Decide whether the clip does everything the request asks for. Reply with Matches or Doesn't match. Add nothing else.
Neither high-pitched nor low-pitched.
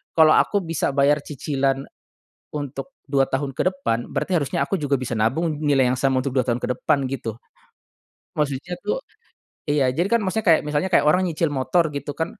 Matches